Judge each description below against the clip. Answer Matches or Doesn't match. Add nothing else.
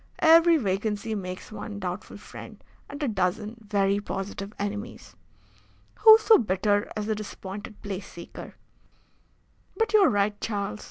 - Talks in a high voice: Matches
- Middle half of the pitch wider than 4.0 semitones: Doesn't match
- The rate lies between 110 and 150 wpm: Matches